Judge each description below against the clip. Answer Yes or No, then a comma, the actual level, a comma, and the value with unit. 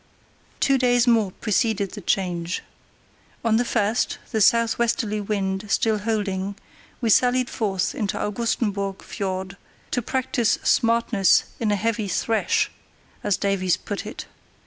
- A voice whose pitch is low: No, high, 215 Hz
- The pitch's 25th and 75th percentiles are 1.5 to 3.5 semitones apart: Yes, average, 2.8 semitones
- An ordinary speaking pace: No, slow, 125 wpm